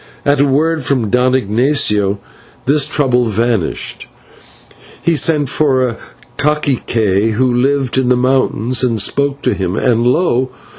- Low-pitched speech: Yes, low, 130 Hz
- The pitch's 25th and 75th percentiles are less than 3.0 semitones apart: No, average, 3.6 semitones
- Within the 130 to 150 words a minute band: Yes, average, 140 wpm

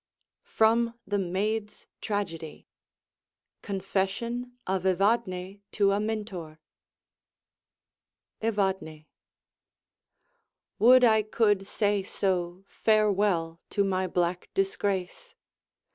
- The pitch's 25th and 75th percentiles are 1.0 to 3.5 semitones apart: Yes, average, 2.7 semitones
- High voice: Yes, high, 200 Hz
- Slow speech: Yes, slow, 75 wpm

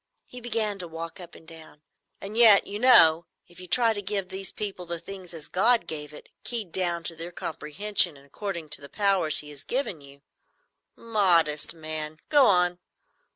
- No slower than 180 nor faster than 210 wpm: Yes, average, 190 wpm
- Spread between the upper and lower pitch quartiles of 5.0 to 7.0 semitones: No, average, 4.4 semitones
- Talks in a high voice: No, medium, 180 Hz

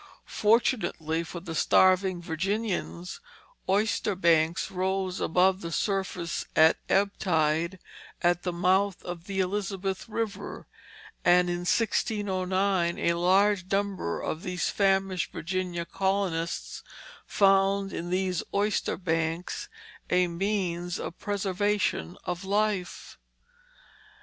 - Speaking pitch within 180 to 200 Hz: Yes, medium, 185 Hz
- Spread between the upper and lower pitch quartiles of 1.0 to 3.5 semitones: Yes, narrow, 2.4 semitones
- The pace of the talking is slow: Yes, slow, 105 wpm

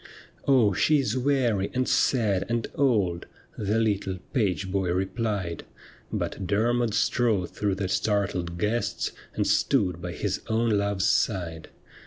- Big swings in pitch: No, average, 3.9 semitones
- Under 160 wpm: Yes, average, 140 wpm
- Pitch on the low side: Yes, low, 100 Hz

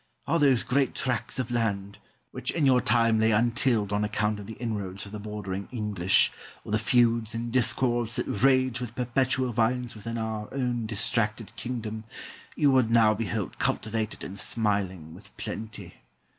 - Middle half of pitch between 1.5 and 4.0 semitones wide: Yes, narrow, 2.5 semitones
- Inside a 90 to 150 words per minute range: No, average, 165 wpm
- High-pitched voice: No, low, 115 Hz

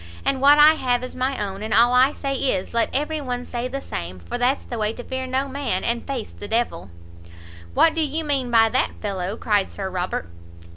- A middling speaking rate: No, fast, 230 wpm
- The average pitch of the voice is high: Yes, high, 245 Hz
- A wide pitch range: No, average, 4.5 semitones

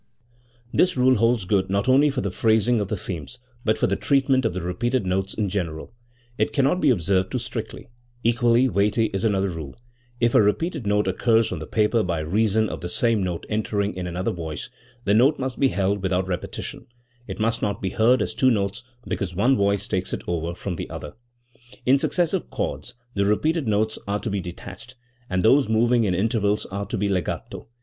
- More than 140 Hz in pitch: No, low, 105 Hz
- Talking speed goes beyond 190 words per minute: Yes, fast, 205 wpm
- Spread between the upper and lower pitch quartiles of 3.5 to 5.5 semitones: Yes, average, 4.1 semitones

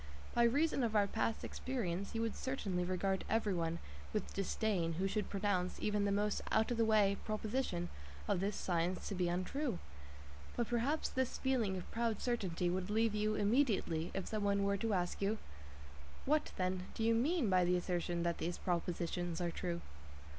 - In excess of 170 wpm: Yes, average, 180 wpm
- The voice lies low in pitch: No, high, 200 Hz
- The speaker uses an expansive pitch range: No, average, 4.0 semitones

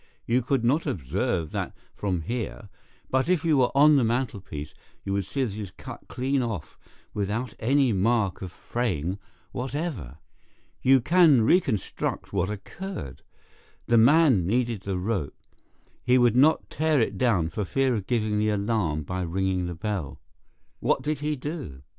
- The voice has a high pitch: No, low, 115 Hz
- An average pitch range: No, wide, 5.8 semitones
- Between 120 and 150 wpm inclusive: No, average, 160 wpm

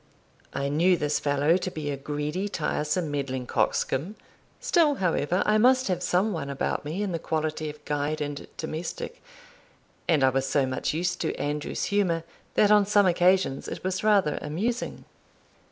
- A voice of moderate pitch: Yes, medium, 160 Hz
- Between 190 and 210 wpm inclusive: No, average, 170 wpm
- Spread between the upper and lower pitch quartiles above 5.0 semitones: No, average, 4.5 semitones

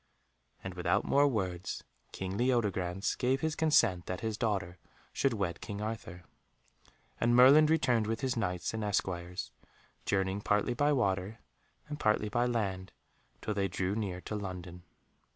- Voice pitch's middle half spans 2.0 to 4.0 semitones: No, average, 4.4 semitones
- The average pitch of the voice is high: No, low, 105 Hz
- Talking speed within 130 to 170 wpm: Yes, average, 150 wpm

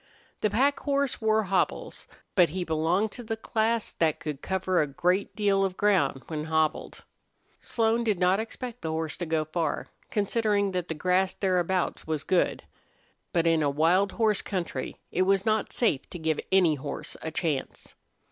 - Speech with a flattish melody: No, average, 4.7 semitones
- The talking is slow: No, average, 175 wpm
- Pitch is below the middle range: No, medium, 185 Hz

